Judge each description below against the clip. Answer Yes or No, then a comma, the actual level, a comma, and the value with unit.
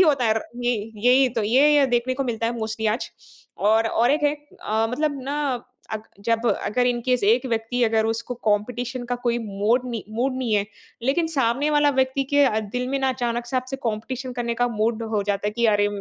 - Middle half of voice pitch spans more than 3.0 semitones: No, average, 2.7 semitones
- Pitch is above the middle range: Yes, high, 240 Hz